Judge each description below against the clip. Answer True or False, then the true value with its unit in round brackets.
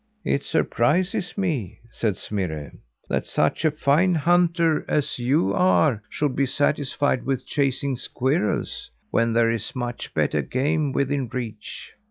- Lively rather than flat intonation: False (4.8 semitones)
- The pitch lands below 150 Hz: True (140 Hz)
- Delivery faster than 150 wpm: False (135 wpm)